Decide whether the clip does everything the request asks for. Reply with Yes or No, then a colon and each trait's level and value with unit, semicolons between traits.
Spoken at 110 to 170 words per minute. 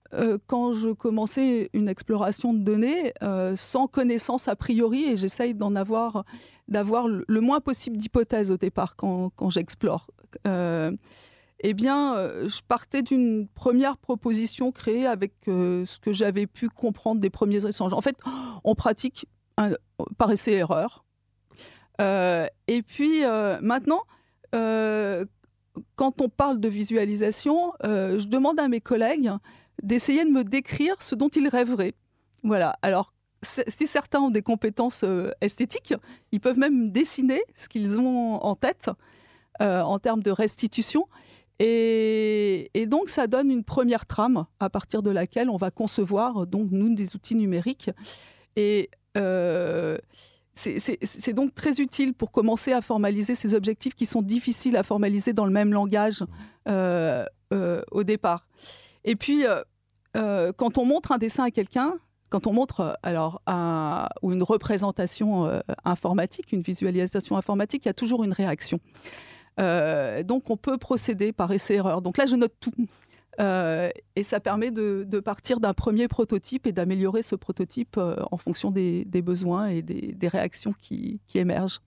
Yes: average, 160 wpm